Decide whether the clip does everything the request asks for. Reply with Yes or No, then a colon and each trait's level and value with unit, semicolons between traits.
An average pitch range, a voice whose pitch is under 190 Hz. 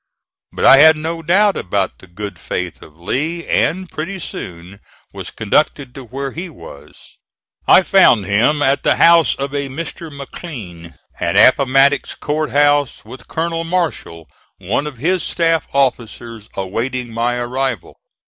No: wide, 6.2 semitones; low, 135 Hz